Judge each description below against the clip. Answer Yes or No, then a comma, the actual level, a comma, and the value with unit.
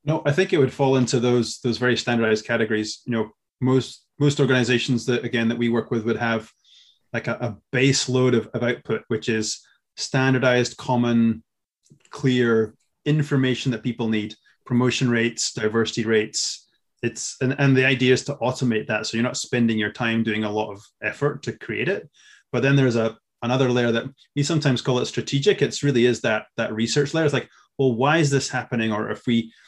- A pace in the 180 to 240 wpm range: Yes, average, 200 wpm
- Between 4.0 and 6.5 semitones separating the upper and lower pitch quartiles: No, narrow, 2.5 semitones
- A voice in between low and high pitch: No, low, 120 Hz